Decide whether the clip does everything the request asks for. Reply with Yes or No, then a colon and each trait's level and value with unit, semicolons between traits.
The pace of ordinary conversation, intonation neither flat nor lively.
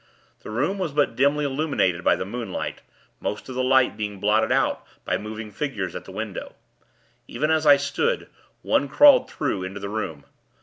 No: average, 180 wpm; wide, 5.8 semitones